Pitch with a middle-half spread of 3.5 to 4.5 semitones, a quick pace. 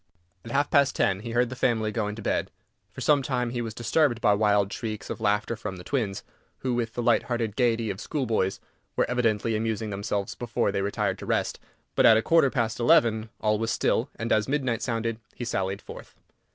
No: narrow, 2.5 semitones; fast, 210 wpm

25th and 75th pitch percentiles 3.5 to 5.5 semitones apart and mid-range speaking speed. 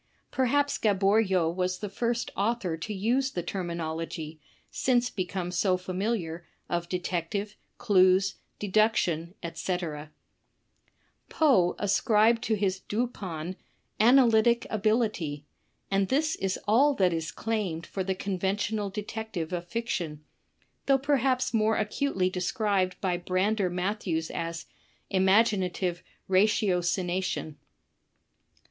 No: average, 3.8 semitones; slow, 110 wpm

